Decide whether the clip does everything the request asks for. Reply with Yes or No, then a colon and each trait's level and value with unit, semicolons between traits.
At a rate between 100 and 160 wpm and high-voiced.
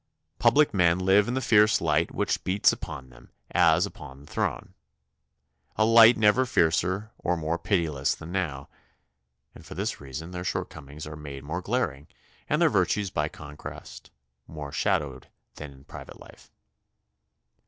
No: average, 155 wpm; very low, 85 Hz